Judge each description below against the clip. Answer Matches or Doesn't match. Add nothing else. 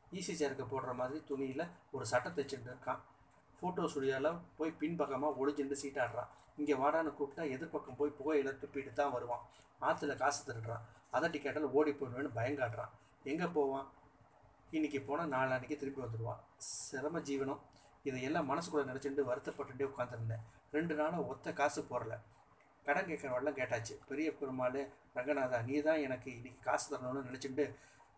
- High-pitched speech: Doesn't match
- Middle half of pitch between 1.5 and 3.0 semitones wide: Matches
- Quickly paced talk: Matches